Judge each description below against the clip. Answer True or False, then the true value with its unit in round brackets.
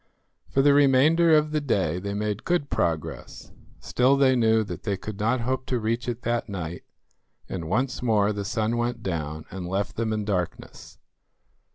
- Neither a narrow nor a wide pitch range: True (4.5 semitones)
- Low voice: True (110 Hz)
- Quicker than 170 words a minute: True (180 wpm)